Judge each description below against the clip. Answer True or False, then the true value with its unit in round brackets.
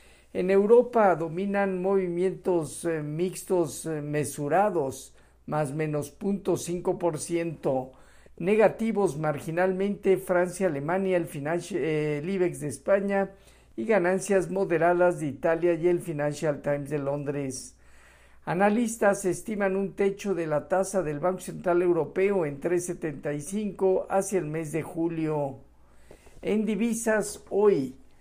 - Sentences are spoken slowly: True (110 wpm)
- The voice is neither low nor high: True (175 Hz)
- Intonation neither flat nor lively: True (4.4 semitones)